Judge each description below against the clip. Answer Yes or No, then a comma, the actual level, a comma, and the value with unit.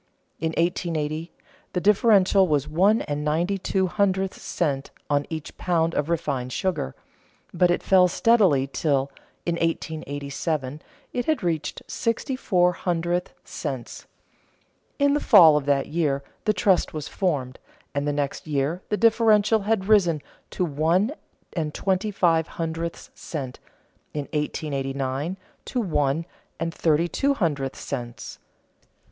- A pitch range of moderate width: Yes, average, 4.6 semitones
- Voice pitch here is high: No, medium, 165 Hz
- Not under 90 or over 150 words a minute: Yes, slow, 135 wpm